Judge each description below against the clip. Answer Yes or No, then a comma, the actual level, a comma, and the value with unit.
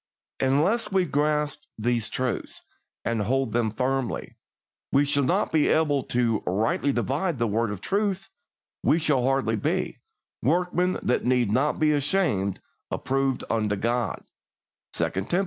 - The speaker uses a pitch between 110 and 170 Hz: Yes, low, 135 Hz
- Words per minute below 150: Yes, average, 140 wpm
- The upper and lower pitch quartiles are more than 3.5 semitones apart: Yes, average, 4.7 semitones